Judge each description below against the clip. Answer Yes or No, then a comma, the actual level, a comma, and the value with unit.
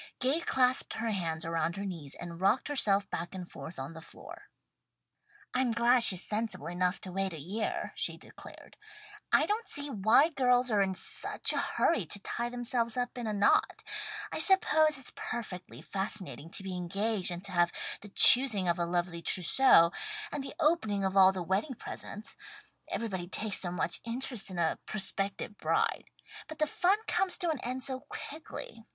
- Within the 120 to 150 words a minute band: No, average, 180 wpm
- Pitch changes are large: Yes, wide, 5.8 semitones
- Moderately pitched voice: No, high, 205 Hz